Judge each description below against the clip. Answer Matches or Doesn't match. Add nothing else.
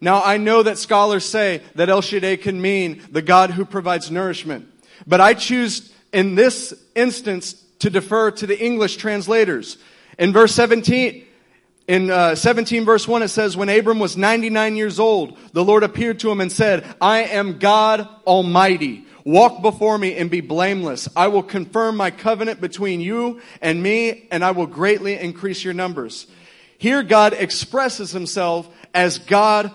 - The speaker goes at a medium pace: Matches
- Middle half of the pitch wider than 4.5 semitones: Doesn't match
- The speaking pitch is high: Matches